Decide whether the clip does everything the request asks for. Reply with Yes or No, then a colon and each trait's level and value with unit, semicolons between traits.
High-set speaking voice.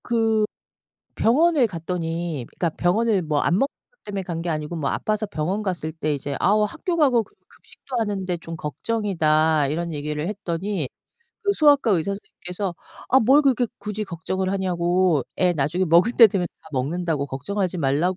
No: medium, 180 Hz